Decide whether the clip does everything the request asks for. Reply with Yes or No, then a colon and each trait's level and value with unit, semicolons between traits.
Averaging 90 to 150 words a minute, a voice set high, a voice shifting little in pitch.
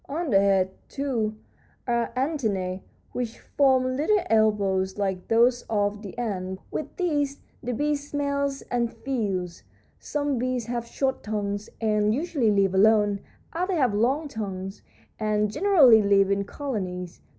No: average, 140 wpm; high, 225 Hz; wide, 5.4 semitones